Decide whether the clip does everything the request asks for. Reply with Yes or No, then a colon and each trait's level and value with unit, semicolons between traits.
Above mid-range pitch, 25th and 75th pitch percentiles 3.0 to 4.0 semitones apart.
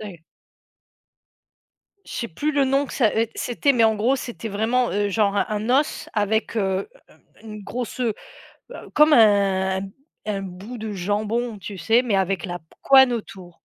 Yes: high, 215 Hz; average, 3.6 semitones